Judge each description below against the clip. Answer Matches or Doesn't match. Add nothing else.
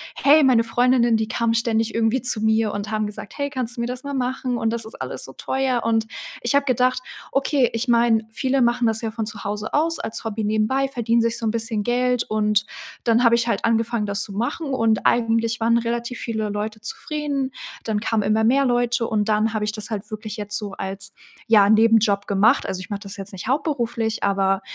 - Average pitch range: Doesn't match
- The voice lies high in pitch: Matches